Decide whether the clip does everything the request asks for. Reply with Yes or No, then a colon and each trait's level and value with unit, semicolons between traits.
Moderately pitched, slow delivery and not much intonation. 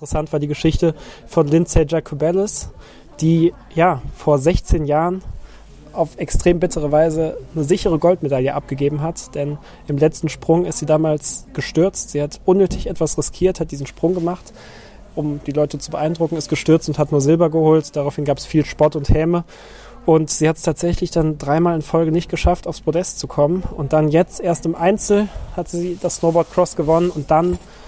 No: medium, 160 Hz; average, 185 wpm; narrow, 2.3 semitones